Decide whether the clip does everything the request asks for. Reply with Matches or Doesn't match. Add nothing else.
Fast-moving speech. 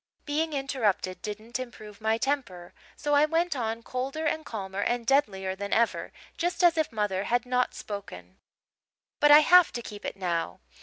Doesn't match